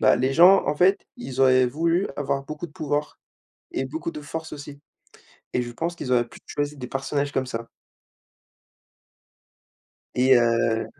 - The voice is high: No, medium, 140 Hz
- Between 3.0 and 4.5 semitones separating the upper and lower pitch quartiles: Yes, average, 3.4 semitones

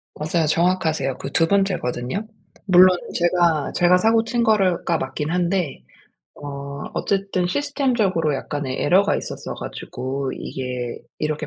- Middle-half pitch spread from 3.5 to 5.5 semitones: Yes, average, 5.2 semitones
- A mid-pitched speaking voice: Yes, medium, 175 Hz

